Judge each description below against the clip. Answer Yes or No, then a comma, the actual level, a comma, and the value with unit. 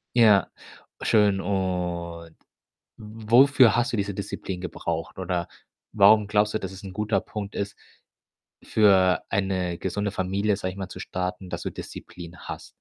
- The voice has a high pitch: No, low, 100 Hz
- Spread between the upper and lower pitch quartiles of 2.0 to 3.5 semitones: Yes, narrow, 2.5 semitones